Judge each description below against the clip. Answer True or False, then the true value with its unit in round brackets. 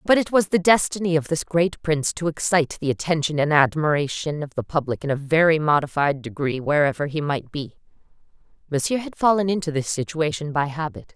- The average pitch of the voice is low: False (155 Hz)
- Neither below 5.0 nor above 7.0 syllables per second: True (5.8 syllables/s)